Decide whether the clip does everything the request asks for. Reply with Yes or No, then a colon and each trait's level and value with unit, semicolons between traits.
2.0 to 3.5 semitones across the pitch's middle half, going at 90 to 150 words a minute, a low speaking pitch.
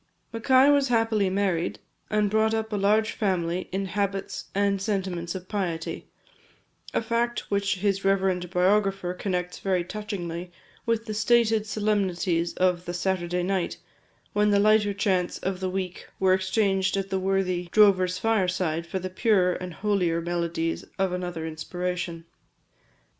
No: narrow, 2.6 semitones; average, 145 wpm; high, 190 Hz